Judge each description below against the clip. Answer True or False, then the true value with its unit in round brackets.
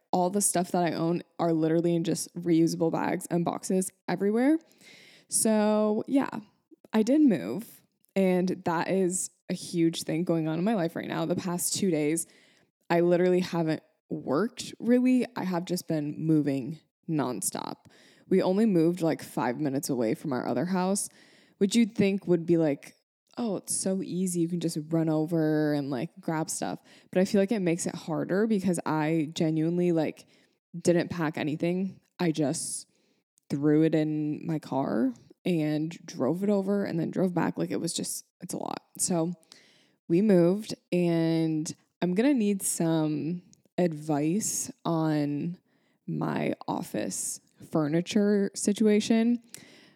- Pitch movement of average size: True (3.4 semitones)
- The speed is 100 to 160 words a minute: True (155 wpm)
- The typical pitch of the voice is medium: True (170 Hz)